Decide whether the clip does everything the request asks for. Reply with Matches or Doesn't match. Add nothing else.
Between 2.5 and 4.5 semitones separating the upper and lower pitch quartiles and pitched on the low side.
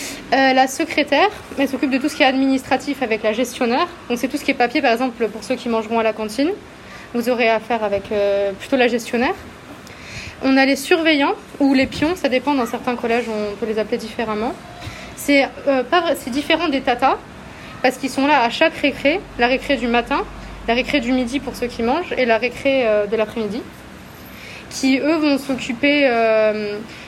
Doesn't match